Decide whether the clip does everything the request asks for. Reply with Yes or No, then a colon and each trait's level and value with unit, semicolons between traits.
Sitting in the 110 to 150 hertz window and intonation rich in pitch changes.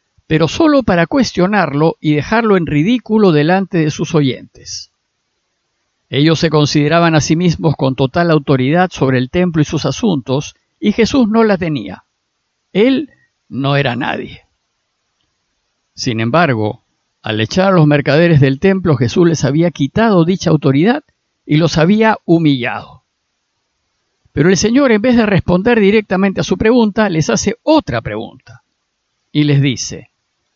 No: medium, 165 Hz; wide, 5.7 semitones